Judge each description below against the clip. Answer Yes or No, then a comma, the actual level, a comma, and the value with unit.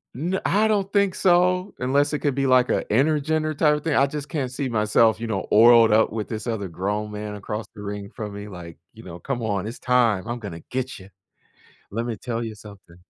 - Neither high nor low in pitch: No, low, 115 Hz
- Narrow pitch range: No, wide, 5.6 semitones